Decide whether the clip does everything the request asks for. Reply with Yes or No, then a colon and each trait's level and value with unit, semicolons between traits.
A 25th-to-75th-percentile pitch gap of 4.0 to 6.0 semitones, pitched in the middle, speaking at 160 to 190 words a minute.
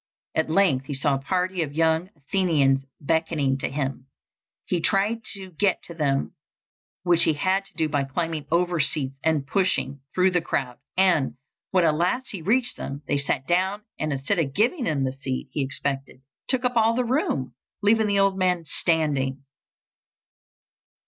Yes: wide, 5.4 semitones; medium, 160 Hz; average, 175 wpm